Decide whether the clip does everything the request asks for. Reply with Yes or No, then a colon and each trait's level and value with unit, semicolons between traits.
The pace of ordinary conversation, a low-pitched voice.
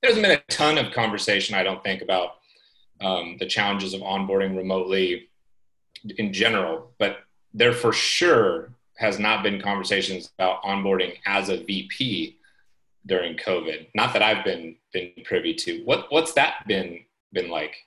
Yes: average, 155 wpm; low, 100 Hz